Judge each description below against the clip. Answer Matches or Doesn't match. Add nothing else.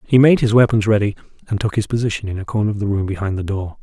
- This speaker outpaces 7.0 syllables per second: Matches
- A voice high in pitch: Doesn't match